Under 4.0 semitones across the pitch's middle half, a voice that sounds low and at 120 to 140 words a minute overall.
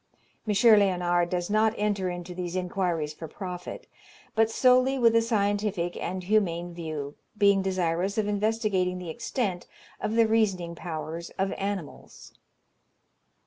No: average, 3.5 semitones; high, 190 Hz; slow, 135 wpm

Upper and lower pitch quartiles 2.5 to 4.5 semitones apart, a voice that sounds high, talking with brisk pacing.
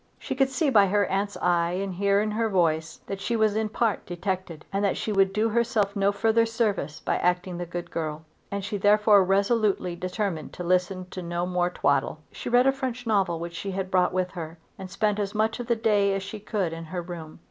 Yes: average, 3.1 semitones; high, 195 Hz; fast, 230 wpm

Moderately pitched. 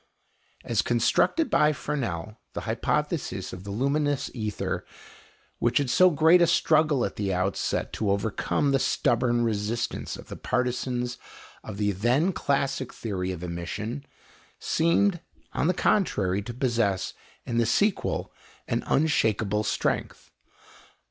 No: low, 120 Hz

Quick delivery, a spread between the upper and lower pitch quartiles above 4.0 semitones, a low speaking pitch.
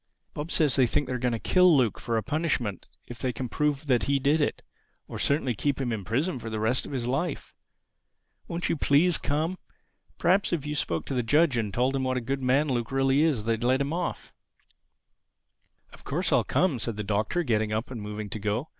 Yes: fast, 225 wpm; average, 4.4 semitones; low, 130 Hz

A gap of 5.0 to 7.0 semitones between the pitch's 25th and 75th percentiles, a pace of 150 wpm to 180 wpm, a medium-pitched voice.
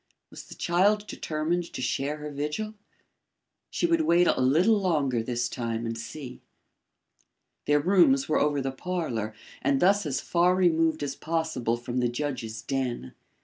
Yes: wide, 5.6 semitones; average, 155 wpm; medium, 145 Hz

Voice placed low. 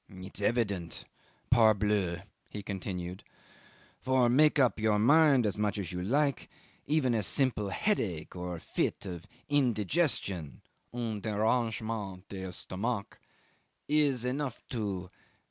Yes: low, 105 Hz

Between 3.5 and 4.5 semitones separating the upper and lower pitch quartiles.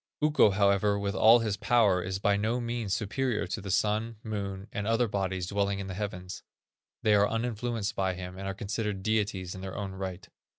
No: narrow, 2.5 semitones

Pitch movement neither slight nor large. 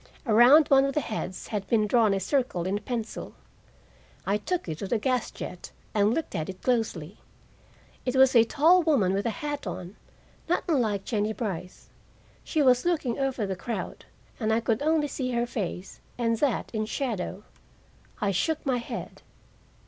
Yes: average, 4.7 semitones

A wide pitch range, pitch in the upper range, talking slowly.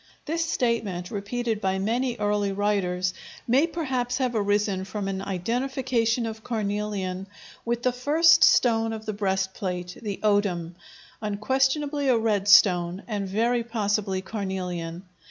No: average, 4.0 semitones; high, 210 Hz; slow, 130 wpm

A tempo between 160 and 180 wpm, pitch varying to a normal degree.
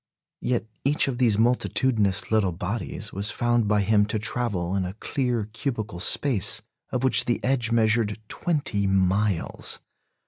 No: average, 145 wpm; average, 3.3 semitones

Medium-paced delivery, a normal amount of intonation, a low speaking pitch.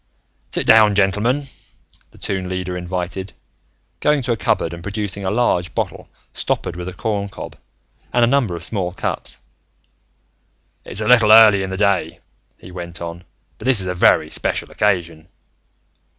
Yes: average, 160 wpm; average, 3.4 semitones; very low, 95 Hz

